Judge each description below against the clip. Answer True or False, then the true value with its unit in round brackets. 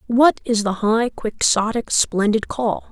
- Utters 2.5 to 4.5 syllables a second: True (3.7 syllables/s)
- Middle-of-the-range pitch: False (225 Hz)